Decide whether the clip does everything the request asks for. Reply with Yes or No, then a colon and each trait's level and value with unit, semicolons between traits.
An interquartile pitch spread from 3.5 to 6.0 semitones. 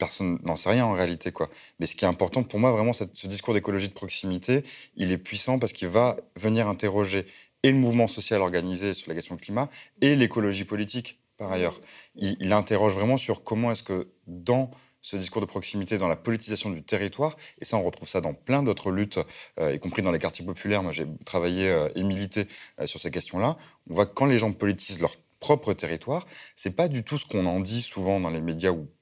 Yes: average, 4.0 semitones